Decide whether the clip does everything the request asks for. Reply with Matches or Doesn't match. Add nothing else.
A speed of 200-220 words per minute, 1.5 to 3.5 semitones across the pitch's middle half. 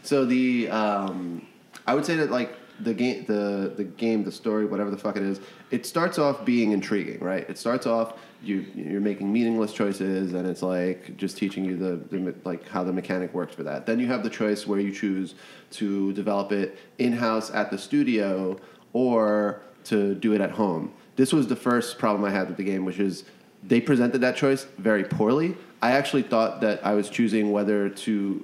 Matches